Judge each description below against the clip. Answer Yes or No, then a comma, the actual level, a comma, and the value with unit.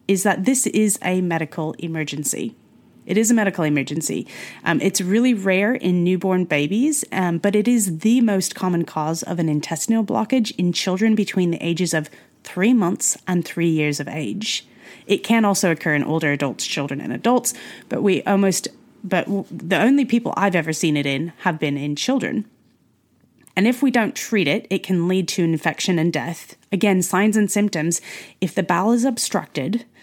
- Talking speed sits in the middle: Yes, average, 185 wpm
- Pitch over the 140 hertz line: Yes, medium, 185 Hz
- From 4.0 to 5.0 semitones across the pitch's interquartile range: Yes, average, 4.7 semitones